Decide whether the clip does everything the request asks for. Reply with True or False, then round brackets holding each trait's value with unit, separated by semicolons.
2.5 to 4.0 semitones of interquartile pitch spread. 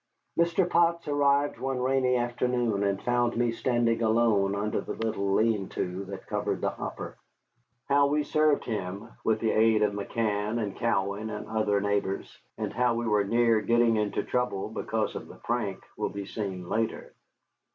True (3.2 semitones)